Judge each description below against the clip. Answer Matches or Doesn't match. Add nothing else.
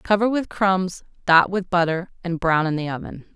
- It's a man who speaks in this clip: Doesn't match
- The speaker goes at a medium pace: Matches